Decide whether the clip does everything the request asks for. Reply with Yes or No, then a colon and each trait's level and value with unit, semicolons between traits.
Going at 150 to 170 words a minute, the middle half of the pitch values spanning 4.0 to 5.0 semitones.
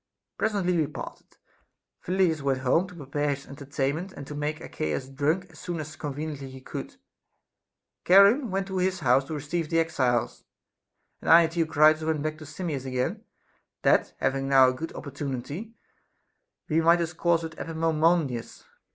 No: average, 165 wpm; average, 3.6 semitones